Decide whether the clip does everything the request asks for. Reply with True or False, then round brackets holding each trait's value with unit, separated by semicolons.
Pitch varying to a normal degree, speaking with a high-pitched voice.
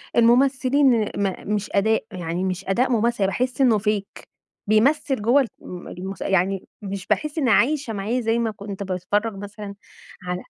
True (3.8 semitones; 210 Hz)